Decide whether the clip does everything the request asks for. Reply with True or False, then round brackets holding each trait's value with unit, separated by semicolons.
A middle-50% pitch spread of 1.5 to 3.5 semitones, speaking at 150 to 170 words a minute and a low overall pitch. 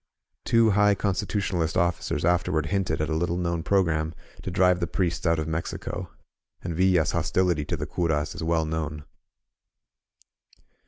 True (2.5 semitones; 160 wpm; 85 Hz)